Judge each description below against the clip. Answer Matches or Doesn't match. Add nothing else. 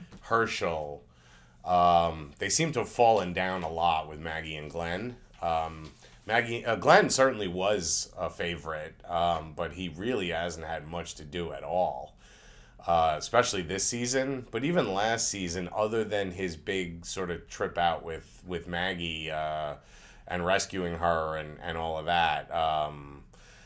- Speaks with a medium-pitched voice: Doesn't match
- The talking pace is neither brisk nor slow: Matches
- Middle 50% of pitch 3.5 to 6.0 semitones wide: Matches